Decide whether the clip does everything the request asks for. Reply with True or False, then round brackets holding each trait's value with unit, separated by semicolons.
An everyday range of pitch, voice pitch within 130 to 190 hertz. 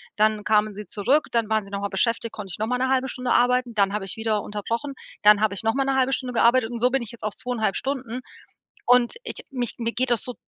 False (3.0 semitones; 230 Hz)